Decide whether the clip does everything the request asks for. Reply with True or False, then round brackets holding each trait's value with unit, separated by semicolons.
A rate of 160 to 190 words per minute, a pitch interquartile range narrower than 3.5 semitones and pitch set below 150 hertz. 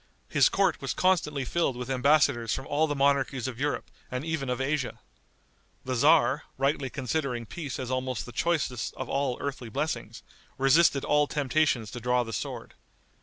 True (170 wpm; 2.9 semitones; 135 Hz)